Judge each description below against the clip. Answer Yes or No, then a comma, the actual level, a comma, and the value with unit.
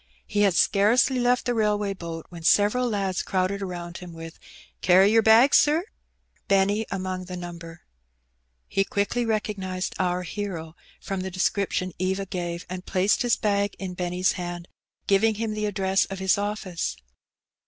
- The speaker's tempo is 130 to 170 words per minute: Yes, average, 155 wpm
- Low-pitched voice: No, high, 195 Hz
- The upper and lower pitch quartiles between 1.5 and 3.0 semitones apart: Yes, narrow, 2.6 semitones